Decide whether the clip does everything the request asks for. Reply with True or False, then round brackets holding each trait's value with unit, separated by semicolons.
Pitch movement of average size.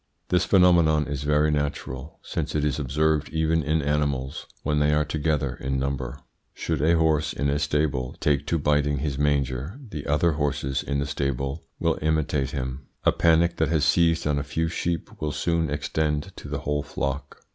False (2.0 semitones)